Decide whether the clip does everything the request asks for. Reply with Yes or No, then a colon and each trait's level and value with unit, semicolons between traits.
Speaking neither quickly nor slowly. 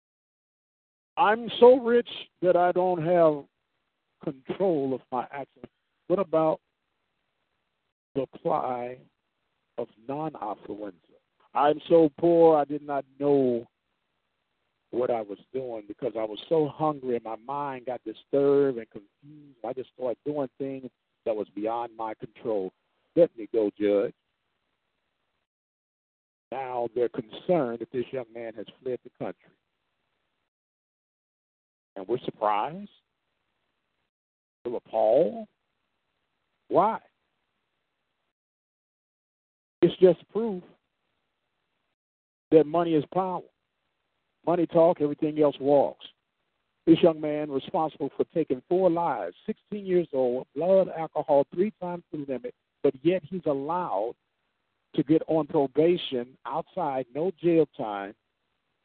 No: slow, 115 wpm